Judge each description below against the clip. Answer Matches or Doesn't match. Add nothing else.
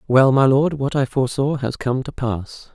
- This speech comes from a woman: Doesn't match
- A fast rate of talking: Matches